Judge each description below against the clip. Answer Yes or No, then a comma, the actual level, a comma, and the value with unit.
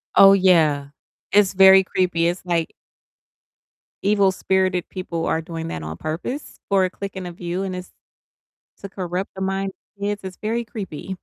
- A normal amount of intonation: No, narrow, 2.2 semitones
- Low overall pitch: No, medium, 185 Hz